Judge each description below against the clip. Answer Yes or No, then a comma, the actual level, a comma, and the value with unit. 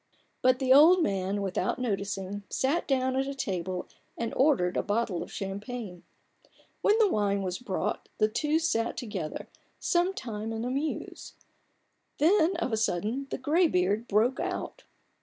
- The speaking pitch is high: Yes, high, 230 Hz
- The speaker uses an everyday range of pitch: No, wide, 5.8 semitones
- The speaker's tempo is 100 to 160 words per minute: Yes, average, 155 wpm